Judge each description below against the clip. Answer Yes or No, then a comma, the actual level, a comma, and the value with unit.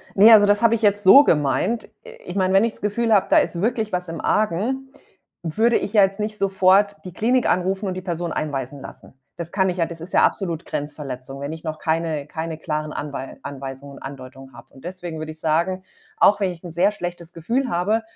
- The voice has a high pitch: No, medium, 175 Hz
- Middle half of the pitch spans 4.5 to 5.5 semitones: Yes, average, 4.8 semitones